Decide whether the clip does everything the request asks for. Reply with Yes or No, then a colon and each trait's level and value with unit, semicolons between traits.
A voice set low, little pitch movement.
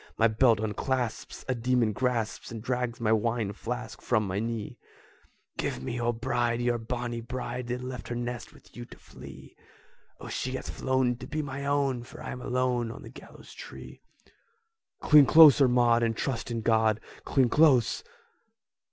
Yes: low, 120 Hz; narrow, 1.8 semitones